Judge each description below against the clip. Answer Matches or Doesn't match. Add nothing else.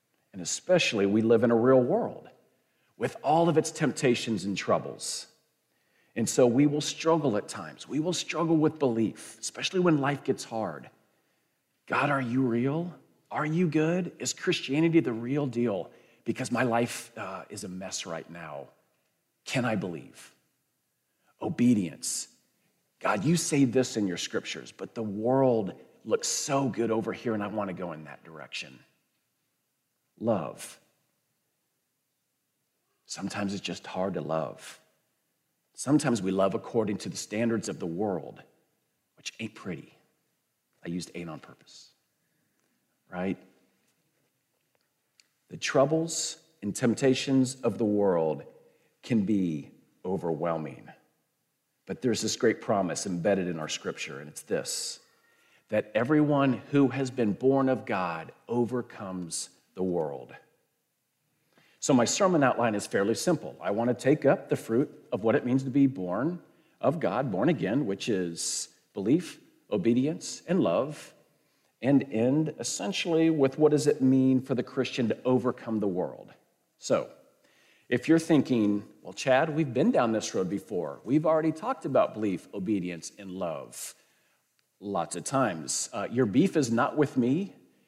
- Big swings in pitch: Matches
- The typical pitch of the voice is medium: Doesn't match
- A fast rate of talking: Doesn't match